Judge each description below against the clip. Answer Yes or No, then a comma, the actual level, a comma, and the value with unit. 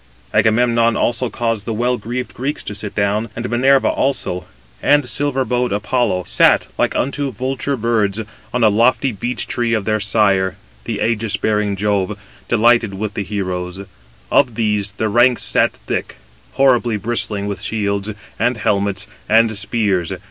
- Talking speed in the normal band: Yes, average, 155 wpm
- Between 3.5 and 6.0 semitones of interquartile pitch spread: No, average, 3.1 semitones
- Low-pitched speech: Yes, low, 110 Hz